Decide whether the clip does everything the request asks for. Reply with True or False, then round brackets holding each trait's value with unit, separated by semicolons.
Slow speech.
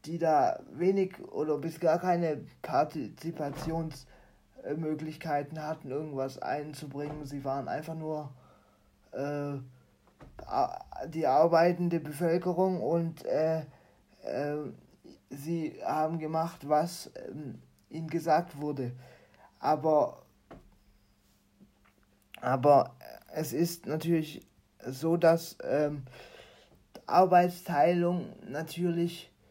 True (80 wpm)